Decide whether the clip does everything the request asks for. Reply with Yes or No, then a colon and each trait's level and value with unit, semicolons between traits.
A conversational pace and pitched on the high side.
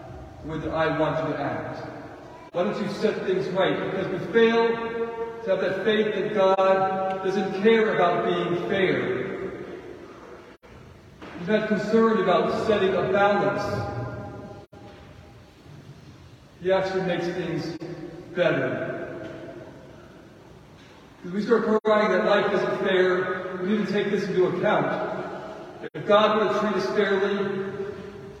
No: slow, 125 wpm; high, 195 Hz